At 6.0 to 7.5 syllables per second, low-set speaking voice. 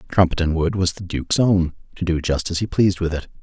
Yes: 6.2 syllables/s; very low, 85 Hz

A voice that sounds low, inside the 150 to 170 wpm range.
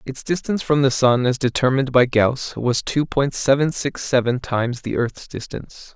No: low, 130 Hz; average, 190 wpm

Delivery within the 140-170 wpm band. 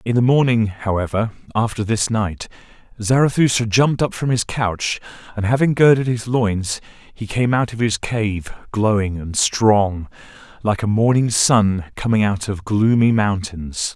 Yes: average, 155 wpm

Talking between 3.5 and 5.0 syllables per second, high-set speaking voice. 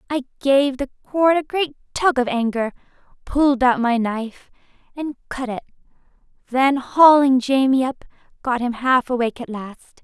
Yes: 4.9 syllables/s; very high, 260 Hz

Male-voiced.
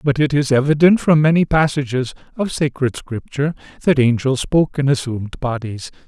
Yes: male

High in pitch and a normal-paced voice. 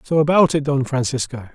No: medium, 140 Hz; average, 195 wpm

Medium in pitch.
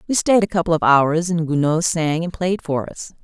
Yes: medium, 165 Hz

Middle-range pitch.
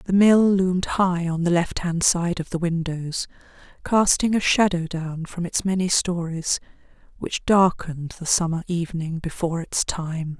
Yes: medium, 175 Hz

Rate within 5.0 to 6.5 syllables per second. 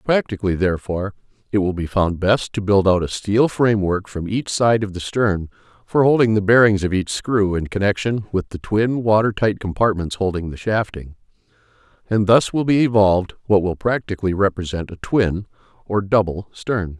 Yes: 5.2 syllables/s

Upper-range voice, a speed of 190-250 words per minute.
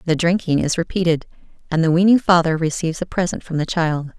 No: medium, 170 Hz; average, 200 wpm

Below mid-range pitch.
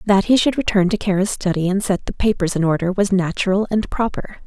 No: high, 195 Hz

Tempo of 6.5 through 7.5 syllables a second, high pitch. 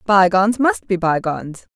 No: 5.1 syllables/s; high, 200 Hz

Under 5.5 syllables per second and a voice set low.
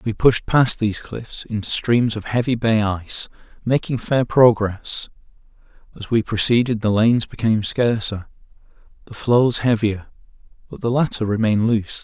Yes: 4.9 syllables/s; low, 115 Hz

